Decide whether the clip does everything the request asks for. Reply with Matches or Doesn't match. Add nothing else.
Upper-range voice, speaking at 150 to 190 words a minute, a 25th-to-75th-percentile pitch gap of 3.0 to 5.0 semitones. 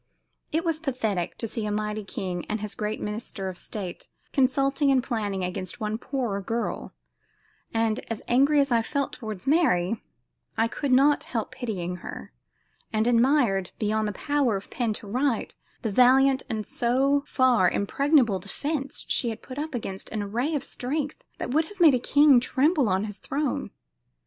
Matches